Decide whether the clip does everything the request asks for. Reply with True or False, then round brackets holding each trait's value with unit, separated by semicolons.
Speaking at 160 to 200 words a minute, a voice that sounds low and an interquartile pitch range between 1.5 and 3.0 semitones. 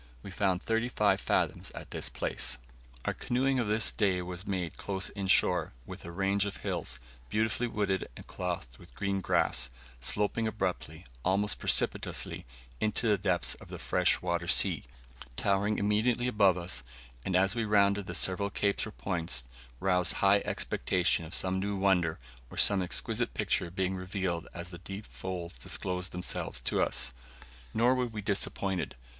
True (165 wpm; 95 Hz; 2.5 semitones)